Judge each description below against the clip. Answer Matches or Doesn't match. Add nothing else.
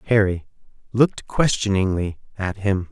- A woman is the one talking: Doesn't match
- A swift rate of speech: Doesn't match